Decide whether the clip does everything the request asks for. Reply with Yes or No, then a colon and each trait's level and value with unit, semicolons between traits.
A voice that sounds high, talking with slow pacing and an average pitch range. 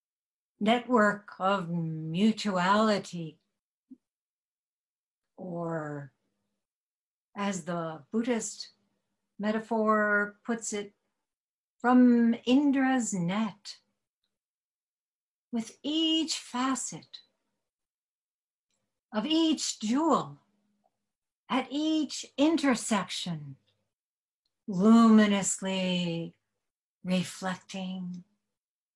Yes: high, 210 Hz; slow, 50 wpm; average, 5.0 semitones